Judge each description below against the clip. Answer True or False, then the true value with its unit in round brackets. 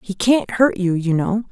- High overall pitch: True (205 Hz)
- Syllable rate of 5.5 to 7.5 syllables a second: False (4.4 syllables/s)